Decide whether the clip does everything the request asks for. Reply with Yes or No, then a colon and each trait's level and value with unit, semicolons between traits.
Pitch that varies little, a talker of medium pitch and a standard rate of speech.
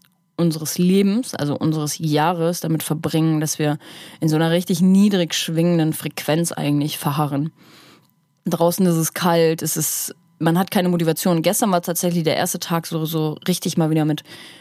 Yes: narrow, 2.1 semitones; medium, 165 Hz; average, 160 wpm